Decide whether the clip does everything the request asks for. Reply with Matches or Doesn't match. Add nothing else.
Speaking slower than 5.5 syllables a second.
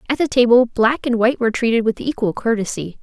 Doesn't match